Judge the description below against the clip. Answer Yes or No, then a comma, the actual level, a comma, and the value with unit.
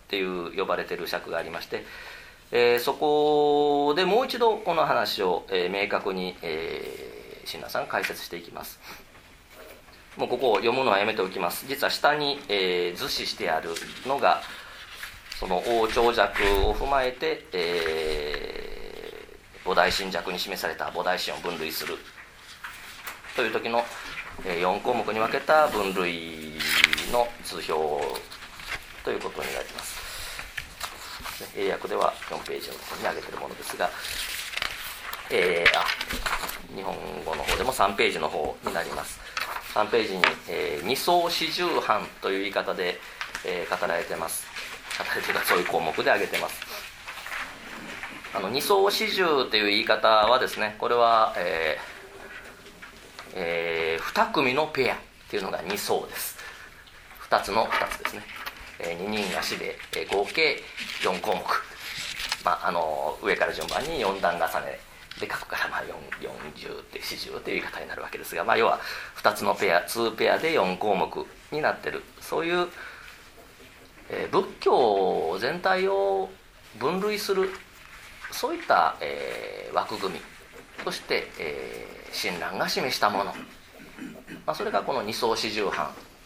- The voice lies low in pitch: No, high, 245 Hz